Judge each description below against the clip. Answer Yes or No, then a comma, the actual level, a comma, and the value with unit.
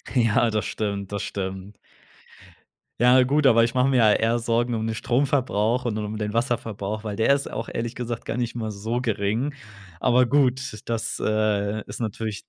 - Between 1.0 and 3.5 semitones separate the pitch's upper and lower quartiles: Yes, narrow, 2.6 semitones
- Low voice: Yes, low, 115 Hz